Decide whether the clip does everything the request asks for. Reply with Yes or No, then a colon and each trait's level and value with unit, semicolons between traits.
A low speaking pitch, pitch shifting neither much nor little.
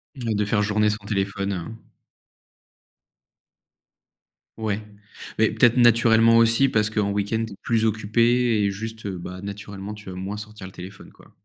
No: low, 105 Hz; narrow, 2.0 semitones